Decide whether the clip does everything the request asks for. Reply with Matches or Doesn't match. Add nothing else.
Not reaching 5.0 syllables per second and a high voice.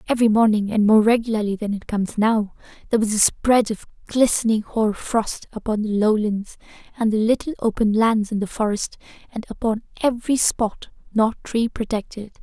Doesn't match